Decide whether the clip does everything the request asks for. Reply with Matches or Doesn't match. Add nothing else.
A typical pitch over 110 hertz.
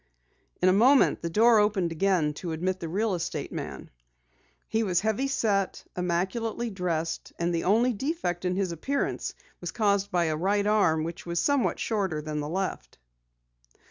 Matches